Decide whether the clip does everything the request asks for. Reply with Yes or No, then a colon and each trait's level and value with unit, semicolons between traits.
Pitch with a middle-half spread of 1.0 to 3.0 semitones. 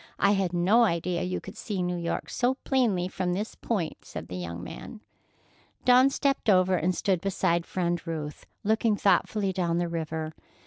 No: average, 3.5 semitones